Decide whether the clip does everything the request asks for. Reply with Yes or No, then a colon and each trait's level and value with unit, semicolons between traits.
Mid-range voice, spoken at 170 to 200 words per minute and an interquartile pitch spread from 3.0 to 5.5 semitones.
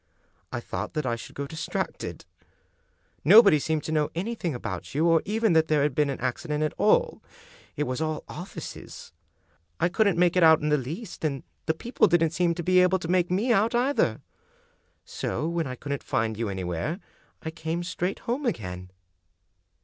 Yes: medium, 160 Hz; average, 190 wpm; average, 4.0 semitones